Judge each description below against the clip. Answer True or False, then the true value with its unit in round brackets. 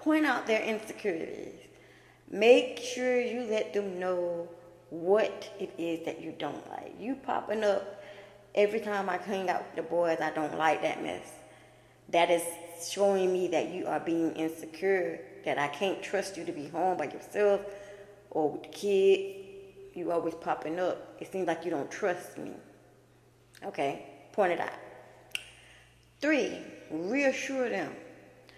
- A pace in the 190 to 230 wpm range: False (155 wpm)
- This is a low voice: False (195 Hz)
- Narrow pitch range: False (4.4 semitones)